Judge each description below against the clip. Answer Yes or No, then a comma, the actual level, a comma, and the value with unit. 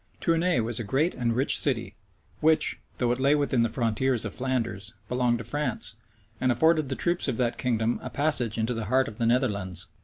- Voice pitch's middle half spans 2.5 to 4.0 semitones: Yes, average, 3.1 semitones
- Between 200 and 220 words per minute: Yes, fast, 205 wpm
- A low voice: Yes, low, 125 Hz